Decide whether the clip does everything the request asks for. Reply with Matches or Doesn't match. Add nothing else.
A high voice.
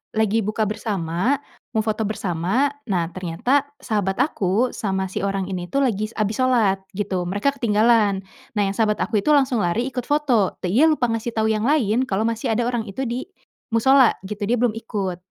Matches